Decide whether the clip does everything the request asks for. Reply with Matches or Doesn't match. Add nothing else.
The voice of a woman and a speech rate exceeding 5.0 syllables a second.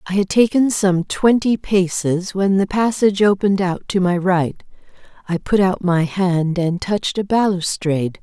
Doesn't match